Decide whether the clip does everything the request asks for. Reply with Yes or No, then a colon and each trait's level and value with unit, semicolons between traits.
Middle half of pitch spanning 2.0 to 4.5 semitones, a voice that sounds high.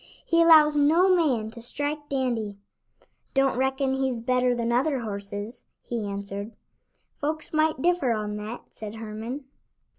No: average, 5.0 semitones; very high, 250 Hz